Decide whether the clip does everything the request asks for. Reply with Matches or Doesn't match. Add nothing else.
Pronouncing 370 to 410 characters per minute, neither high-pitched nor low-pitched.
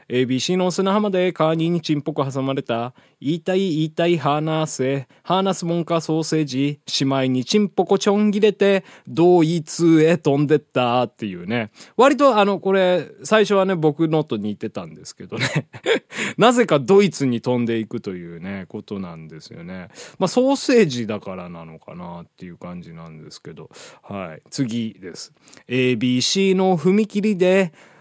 Doesn't match